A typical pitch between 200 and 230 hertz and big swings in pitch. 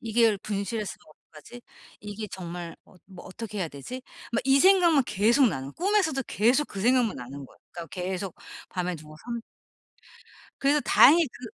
Yes: high, 210 Hz; wide, 6.5 semitones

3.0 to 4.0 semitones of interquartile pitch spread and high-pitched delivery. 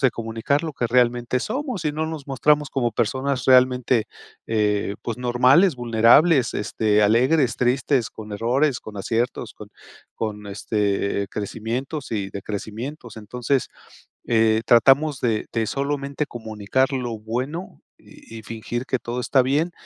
No: average, 3.7 semitones; low, 120 Hz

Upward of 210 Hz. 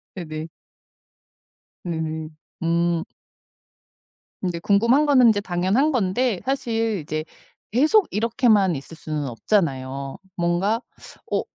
No: medium, 185 Hz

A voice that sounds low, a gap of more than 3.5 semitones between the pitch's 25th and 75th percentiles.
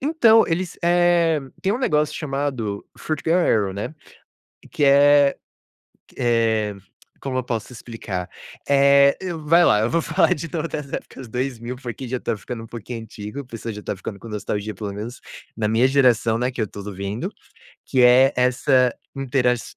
Yes: low, 125 Hz; average, 4.6 semitones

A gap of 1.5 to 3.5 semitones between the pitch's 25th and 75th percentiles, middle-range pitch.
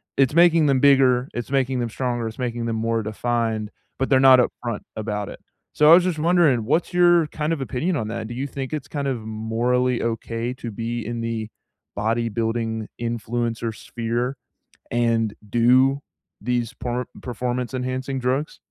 No: average, 2.7 semitones; low, 120 Hz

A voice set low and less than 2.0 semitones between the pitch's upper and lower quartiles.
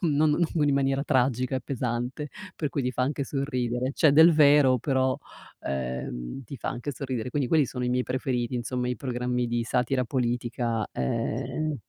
No: low, 130 Hz; narrow, 2.5 semitones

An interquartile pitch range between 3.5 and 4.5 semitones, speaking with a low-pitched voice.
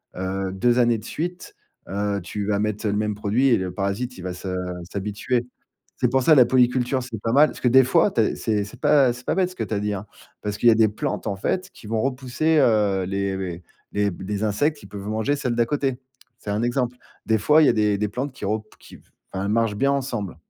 Yes: average, 4.0 semitones; low, 110 Hz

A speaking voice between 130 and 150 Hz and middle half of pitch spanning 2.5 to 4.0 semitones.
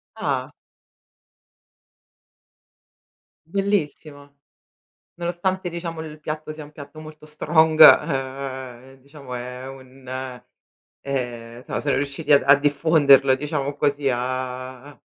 Yes: medium, 140 Hz; average, 2.9 semitones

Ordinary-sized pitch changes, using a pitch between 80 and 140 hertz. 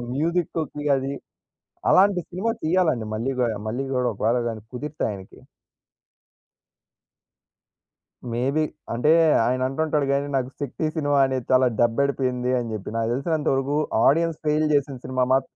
Yes: average, 3.5 semitones; low, 135 Hz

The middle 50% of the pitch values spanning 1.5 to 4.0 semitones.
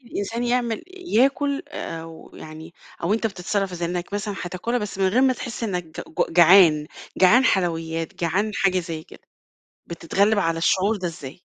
No: average, 4.7 semitones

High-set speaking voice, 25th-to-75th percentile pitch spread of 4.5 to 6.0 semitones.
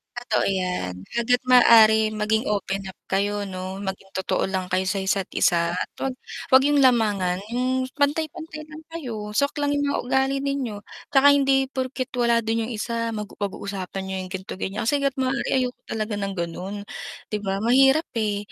Yes: high, 225 Hz; average, 5.3 semitones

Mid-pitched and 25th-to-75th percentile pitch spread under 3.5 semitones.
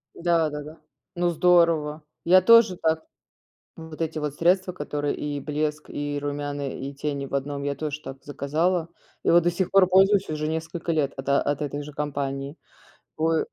Yes: medium, 155 Hz; average, 2.8 semitones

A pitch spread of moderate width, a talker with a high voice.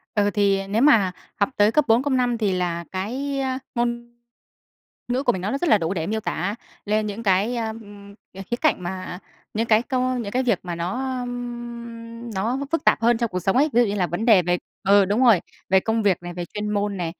Yes: average, 3.8 semitones; high, 220 Hz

